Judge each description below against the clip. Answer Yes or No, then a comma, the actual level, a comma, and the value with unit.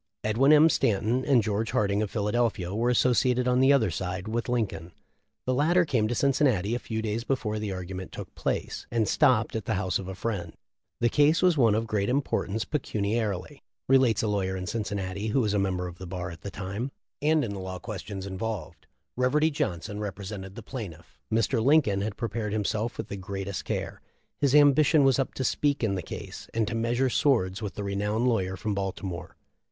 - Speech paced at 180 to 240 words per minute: Yes, average, 200 wpm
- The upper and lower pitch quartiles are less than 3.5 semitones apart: No, average, 4.3 semitones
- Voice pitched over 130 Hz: No, low, 110 Hz